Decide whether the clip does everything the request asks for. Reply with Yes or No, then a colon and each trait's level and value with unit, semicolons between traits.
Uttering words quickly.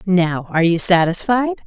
No: average, 145 wpm